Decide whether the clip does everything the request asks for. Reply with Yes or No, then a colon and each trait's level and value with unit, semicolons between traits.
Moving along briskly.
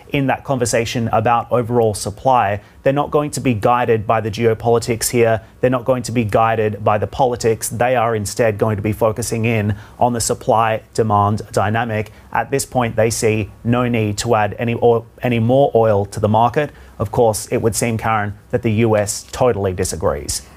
No: average, 195 wpm